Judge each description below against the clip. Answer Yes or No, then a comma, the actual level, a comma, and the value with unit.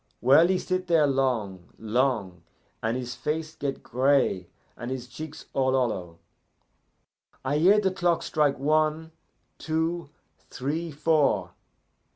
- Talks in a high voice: No, medium, 140 Hz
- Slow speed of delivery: Yes, slow, 125 wpm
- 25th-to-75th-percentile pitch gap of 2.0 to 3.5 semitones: No, average, 4.3 semitones